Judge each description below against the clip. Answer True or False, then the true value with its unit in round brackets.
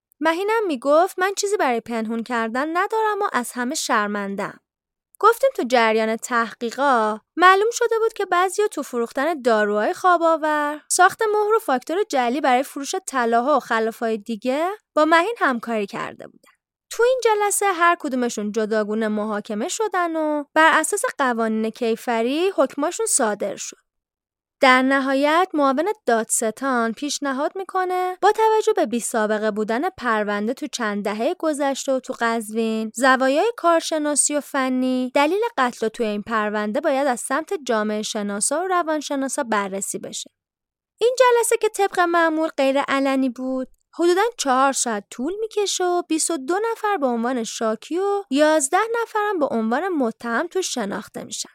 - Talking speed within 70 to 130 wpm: False (145 wpm)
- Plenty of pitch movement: True (7.7 semitones)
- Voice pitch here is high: True (280 Hz)